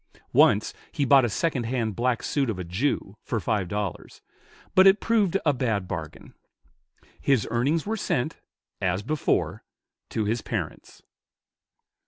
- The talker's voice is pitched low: Yes, low, 120 Hz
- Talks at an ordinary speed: Yes, average, 145 wpm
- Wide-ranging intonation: Yes, wide, 6.0 semitones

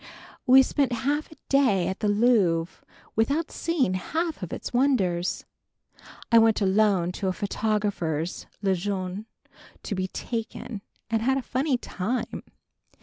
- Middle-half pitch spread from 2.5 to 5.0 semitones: No, wide, 5.4 semitones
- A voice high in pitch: Yes, high, 215 Hz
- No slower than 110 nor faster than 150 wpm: Yes, average, 140 wpm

